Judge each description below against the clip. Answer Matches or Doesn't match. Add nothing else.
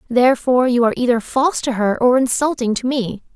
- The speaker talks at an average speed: Matches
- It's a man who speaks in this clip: Doesn't match